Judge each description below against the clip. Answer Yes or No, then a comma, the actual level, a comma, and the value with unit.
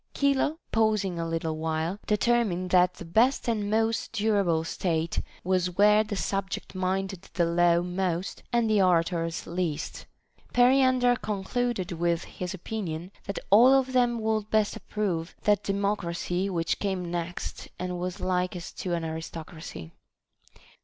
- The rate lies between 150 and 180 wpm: No, average, 140 wpm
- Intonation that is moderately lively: Yes, average, 3.9 semitones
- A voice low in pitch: No, medium, 185 Hz